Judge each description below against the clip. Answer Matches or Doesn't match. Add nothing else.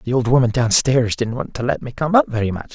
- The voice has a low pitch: Matches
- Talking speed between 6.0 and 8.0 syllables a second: Matches